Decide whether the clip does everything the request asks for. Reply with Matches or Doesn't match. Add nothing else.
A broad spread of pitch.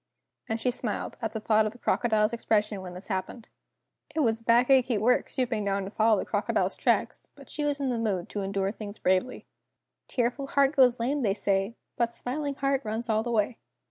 Doesn't match